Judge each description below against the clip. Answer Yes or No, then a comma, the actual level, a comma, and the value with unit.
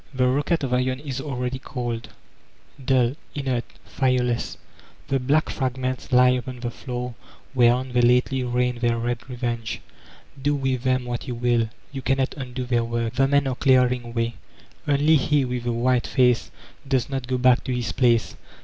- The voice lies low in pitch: Yes, low, 125 Hz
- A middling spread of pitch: No, narrow, 1.5 semitones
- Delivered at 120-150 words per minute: No, average, 175 wpm